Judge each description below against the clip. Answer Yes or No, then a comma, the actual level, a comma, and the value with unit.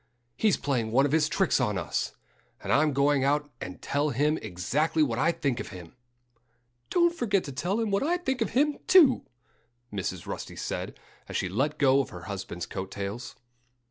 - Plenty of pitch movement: Yes, wide, 8.7 semitones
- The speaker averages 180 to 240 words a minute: Yes, average, 190 wpm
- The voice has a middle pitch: Yes, medium, 145 Hz